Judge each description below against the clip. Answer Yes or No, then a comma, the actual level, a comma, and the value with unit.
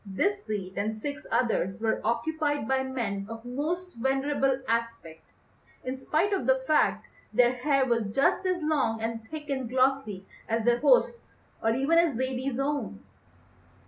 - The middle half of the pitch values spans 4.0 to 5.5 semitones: Yes, average, 4.4 semitones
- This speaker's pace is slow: No, average, 155 wpm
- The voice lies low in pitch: No, very high, 260 Hz